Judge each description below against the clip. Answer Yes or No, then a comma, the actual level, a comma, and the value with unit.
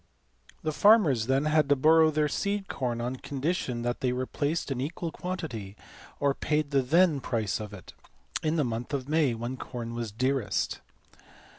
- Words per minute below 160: No, average, 170 wpm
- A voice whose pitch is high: No, low, 135 Hz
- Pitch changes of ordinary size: Yes, average, 4.4 semitones